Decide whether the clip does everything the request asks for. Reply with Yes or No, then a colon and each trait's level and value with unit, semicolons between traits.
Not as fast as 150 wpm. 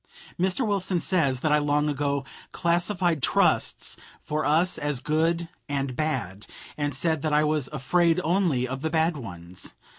No: average, 155 wpm